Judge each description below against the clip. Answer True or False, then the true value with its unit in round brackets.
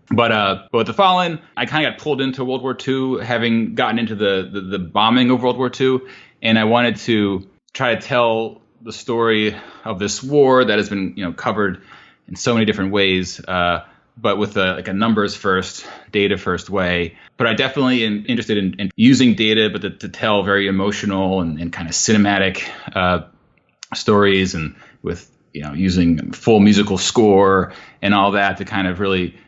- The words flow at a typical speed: True (195 wpm)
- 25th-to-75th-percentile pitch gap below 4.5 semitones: True (4.0 semitones)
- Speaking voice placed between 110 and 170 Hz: False (100 Hz)